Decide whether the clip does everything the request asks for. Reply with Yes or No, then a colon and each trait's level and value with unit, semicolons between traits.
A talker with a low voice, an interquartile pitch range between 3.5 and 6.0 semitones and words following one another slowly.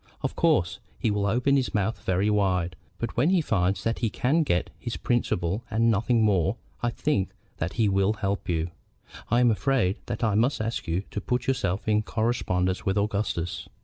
No: low, 105 Hz; average, 3.8 semitones; average, 190 wpm